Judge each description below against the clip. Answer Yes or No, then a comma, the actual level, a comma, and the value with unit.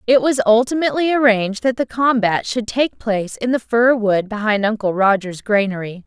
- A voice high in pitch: Yes, high, 225 Hz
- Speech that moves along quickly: No, average, 180 wpm